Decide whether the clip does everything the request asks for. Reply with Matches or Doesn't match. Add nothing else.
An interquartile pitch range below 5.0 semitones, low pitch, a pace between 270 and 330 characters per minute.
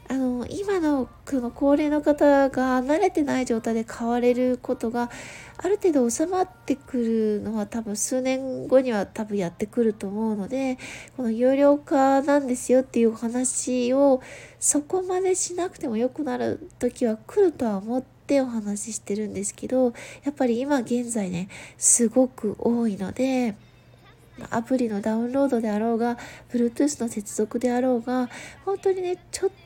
Doesn't match